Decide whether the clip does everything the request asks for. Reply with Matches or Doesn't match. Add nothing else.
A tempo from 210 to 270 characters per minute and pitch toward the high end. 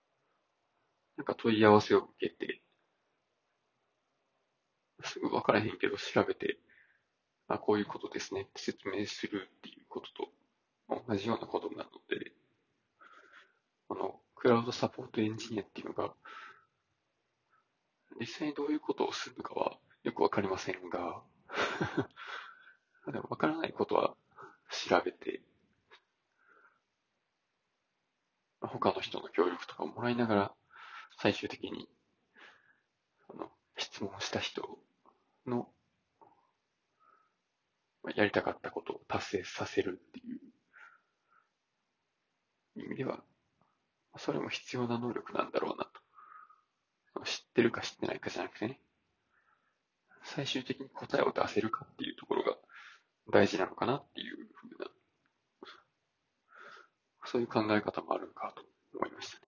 Matches